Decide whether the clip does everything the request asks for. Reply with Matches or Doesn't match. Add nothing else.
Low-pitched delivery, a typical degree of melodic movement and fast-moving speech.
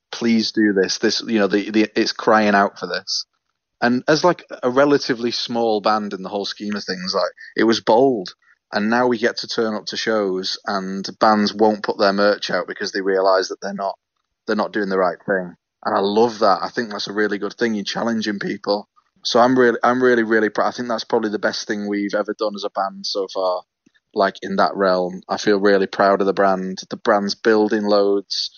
Doesn't match